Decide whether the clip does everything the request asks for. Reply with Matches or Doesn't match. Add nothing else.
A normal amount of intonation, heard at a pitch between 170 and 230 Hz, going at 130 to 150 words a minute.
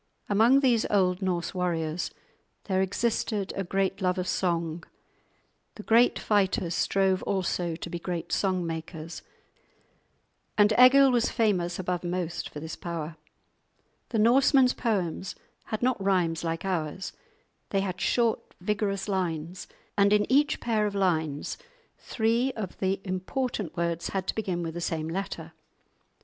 Matches